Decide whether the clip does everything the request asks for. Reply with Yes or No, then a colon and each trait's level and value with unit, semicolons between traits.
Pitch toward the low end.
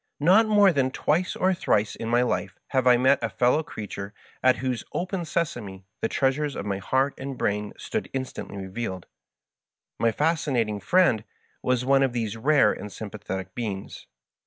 Yes: low, 125 Hz